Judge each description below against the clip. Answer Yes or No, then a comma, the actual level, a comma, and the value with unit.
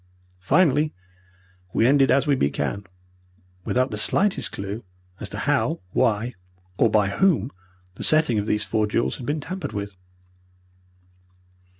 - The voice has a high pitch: No, low, 120 Hz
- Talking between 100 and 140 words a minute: Yes, slow, 135 wpm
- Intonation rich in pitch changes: Yes, wide, 5.9 semitones